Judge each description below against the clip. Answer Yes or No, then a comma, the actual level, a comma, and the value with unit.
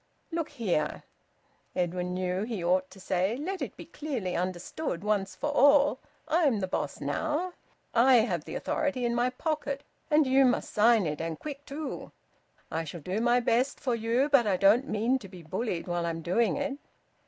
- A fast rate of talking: No, average, 190 wpm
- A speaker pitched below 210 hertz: No, high, 230 Hz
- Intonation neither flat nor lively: No, wide, 7.3 semitones